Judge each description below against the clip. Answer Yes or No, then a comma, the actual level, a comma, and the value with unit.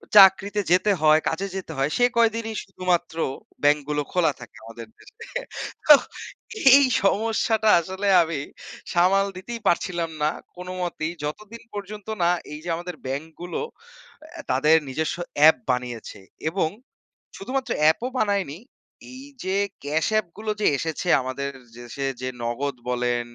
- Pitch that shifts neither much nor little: No, wide, 5.7 semitones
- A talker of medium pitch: Yes, medium, 175 Hz